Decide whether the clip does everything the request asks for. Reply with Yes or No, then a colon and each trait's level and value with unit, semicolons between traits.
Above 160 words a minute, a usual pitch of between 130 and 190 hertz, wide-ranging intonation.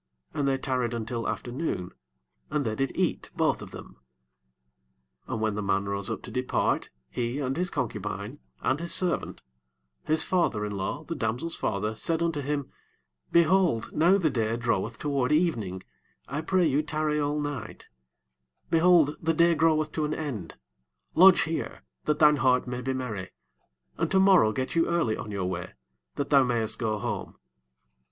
Yes: average, 170 wpm; low, 135 Hz; wide, 6.2 semitones